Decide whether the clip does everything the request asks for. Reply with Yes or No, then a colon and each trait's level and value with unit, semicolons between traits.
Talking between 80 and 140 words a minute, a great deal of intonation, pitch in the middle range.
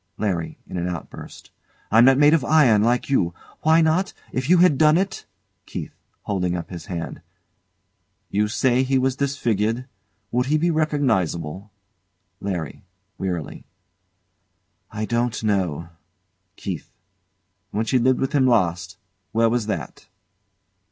No: slow, 135 wpm; wide, 6.7 semitones; low, 115 Hz